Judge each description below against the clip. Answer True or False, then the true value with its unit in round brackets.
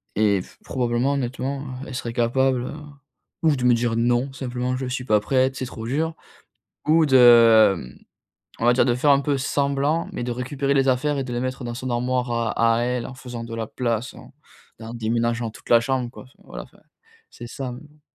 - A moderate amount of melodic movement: False (2.1 semitones)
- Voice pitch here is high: False (125 Hz)